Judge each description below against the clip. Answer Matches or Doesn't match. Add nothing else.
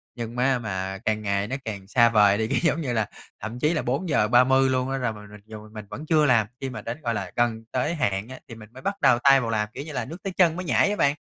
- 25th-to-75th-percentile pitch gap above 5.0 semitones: Doesn't match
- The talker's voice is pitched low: Matches